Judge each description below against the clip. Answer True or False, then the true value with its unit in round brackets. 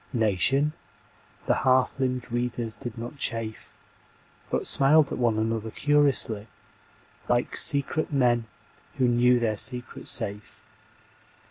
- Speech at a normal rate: False (115 wpm)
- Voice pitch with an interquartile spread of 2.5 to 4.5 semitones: True (3.0 semitones)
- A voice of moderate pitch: False (120 Hz)